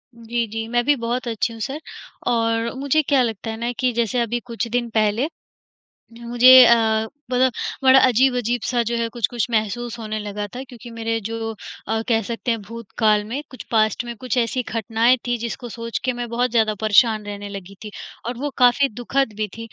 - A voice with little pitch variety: Yes, narrow, 1.8 semitones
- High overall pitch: Yes, high, 235 Hz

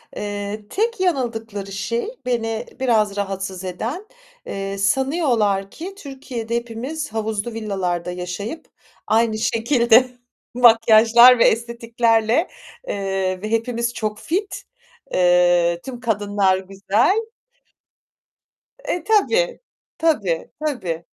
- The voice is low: No, high, 225 Hz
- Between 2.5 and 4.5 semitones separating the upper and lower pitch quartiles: Yes, average, 4.1 semitones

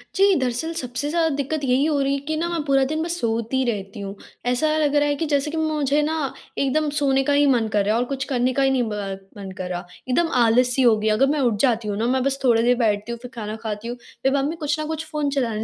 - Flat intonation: No, average, 4.3 semitones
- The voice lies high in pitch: Yes, very high, 265 Hz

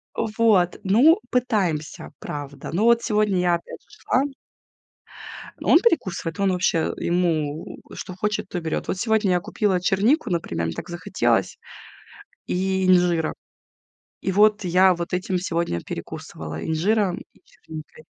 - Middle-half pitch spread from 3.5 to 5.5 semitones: Yes, average, 4.2 semitones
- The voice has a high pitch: No, medium, 180 Hz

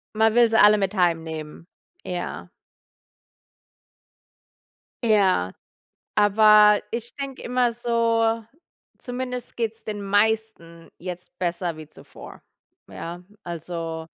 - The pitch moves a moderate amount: Yes, average, 4.7 semitones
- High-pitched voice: Yes, high, 205 Hz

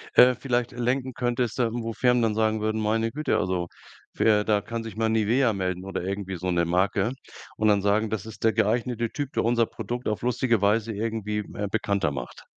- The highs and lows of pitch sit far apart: No, average, 2.7 semitones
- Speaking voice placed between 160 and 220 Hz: No, low, 110 Hz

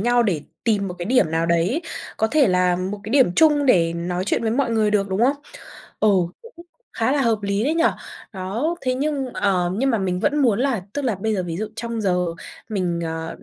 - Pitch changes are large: Yes, wide, 6.1 semitones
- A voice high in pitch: Yes, high, 215 Hz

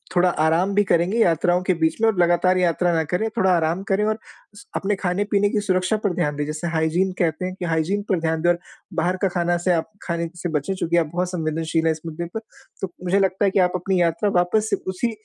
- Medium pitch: Yes, medium, 180 Hz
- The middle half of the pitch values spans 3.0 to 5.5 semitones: No, narrow, 2.6 semitones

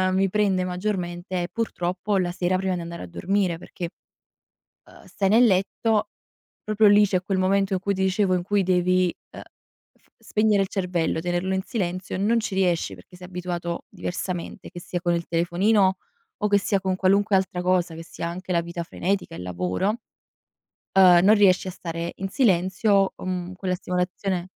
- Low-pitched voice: No, medium, 185 Hz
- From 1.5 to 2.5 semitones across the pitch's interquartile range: Yes, narrow, 2.0 semitones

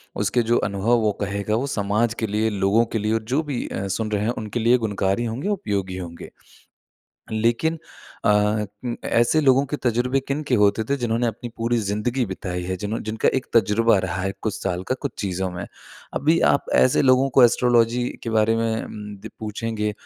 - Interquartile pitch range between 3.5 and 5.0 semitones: No, average, 3.1 semitones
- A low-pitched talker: Yes, low, 110 Hz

